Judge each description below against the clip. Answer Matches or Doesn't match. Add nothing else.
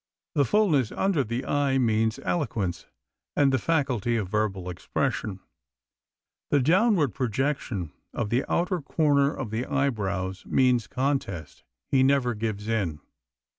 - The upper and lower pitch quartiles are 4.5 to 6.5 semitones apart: Matches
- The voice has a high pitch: Doesn't match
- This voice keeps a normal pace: Doesn't match